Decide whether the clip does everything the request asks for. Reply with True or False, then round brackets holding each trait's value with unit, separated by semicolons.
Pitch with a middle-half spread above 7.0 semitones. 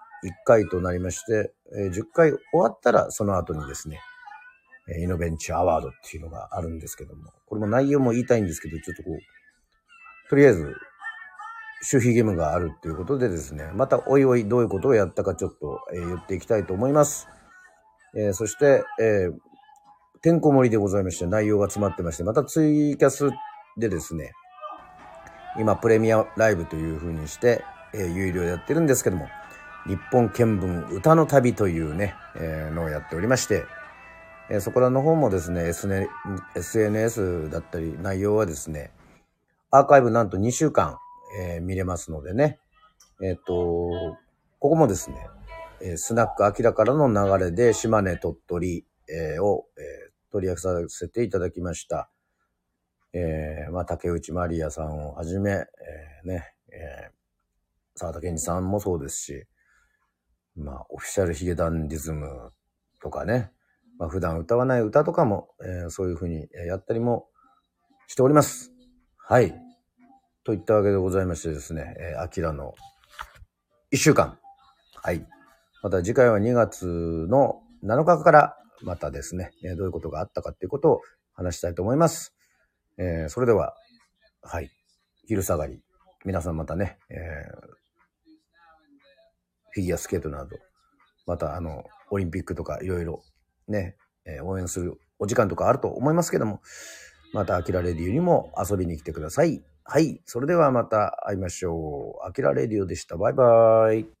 True (7.9 semitones)